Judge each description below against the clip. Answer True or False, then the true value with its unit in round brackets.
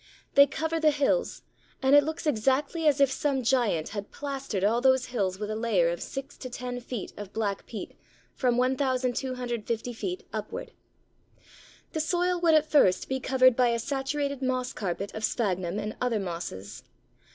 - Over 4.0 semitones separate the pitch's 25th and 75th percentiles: True (4.6 semitones)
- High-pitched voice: True (250 Hz)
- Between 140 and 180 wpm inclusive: True (170 wpm)